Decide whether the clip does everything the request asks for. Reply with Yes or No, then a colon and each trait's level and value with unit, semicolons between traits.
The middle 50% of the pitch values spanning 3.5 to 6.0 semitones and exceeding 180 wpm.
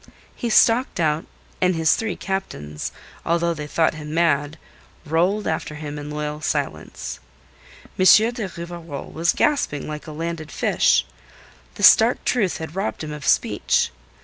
No: average, 3.8 semitones; average, 150 wpm